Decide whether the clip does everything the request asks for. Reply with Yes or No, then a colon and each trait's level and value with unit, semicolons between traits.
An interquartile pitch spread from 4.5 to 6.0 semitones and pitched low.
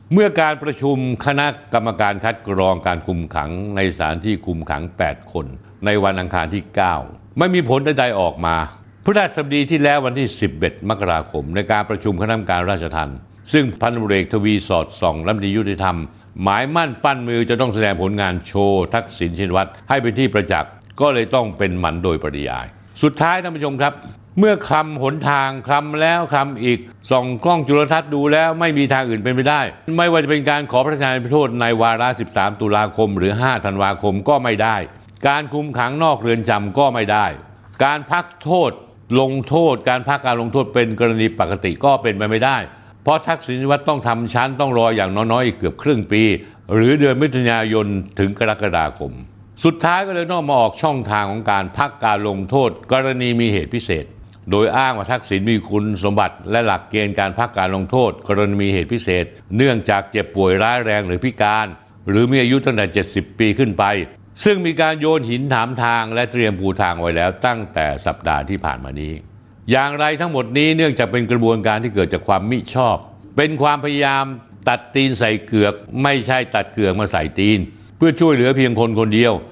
Yes: average, 5.2 semitones; low, 115 Hz